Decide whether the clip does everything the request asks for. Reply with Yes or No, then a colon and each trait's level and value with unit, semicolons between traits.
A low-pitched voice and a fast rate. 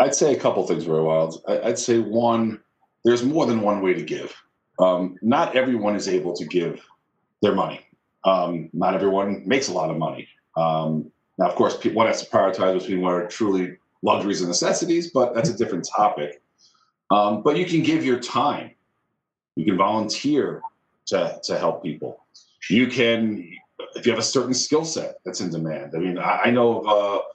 No: low, 105 Hz; average, 190 wpm